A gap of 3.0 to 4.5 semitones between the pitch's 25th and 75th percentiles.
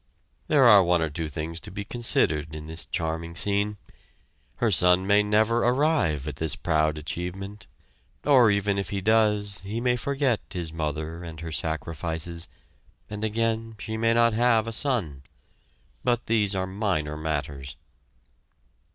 No: wide, 5.6 semitones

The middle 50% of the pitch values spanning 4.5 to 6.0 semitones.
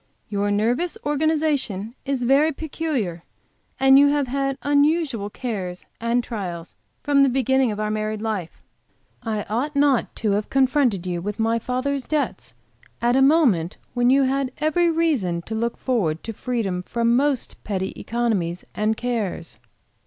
Yes: average, 5.1 semitones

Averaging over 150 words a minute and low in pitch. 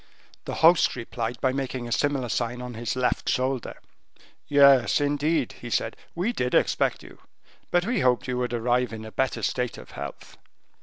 Yes: average, 185 wpm; low, 125 Hz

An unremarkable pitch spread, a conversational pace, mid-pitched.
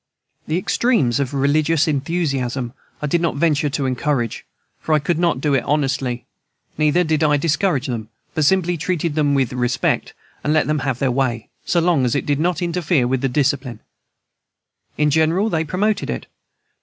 Yes: average, 3.8 semitones; average, 175 wpm; medium, 150 Hz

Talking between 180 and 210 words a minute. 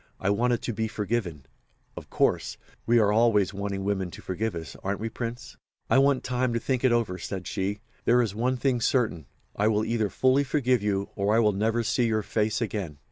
Yes: fast, 205 wpm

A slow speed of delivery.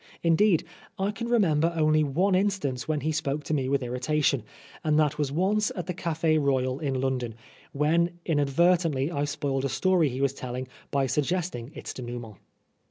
No: average, 175 wpm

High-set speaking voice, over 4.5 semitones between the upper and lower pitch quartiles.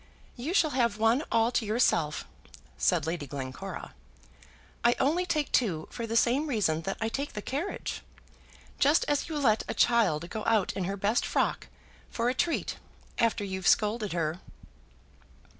Yes: high, 225 Hz; average, 5.1 semitones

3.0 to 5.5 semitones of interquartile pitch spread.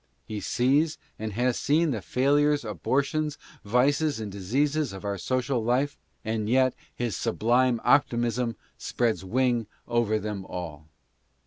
Yes: average, 4.3 semitones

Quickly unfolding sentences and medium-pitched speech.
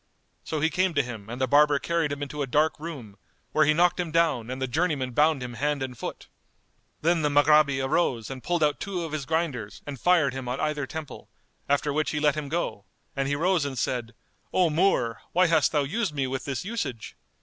Yes: fast, 225 wpm; medium, 145 Hz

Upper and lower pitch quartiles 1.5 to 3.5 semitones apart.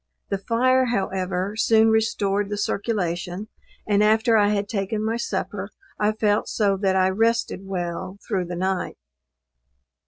Yes: narrow, 2.6 semitones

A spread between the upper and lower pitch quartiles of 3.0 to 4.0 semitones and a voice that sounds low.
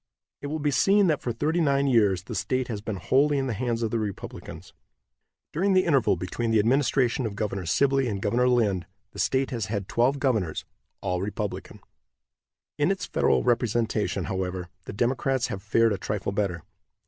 No: average, 5.1 semitones; low, 115 Hz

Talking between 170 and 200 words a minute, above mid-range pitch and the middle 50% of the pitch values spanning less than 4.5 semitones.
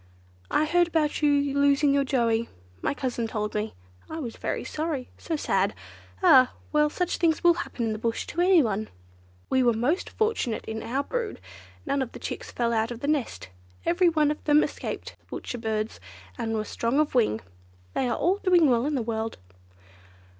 No: average, 190 wpm; very high, 265 Hz; average, 5.3 semitones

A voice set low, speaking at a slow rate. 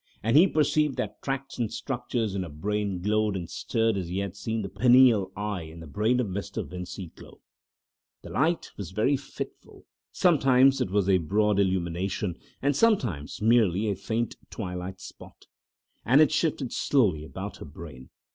No: low, 105 Hz; average, 170 wpm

